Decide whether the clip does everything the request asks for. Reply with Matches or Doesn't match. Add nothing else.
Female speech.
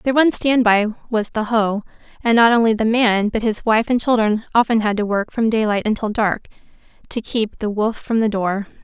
Matches